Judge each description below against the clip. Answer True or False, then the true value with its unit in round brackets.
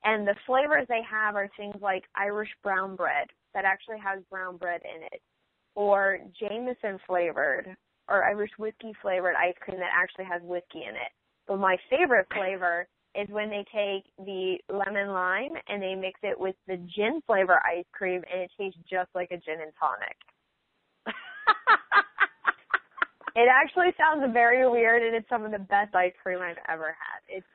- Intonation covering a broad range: False (2.9 semitones)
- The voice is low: False (195 Hz)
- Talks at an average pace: True (175 wpm)